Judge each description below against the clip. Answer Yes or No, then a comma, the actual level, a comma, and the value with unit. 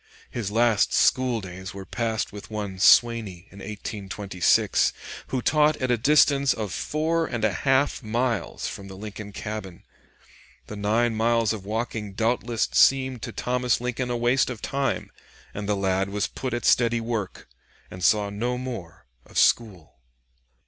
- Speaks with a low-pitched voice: Yes, low, 110 Hz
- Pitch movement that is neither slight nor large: Yes, average, 3.5 semitones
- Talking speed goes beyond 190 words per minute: No, average, 155 wpm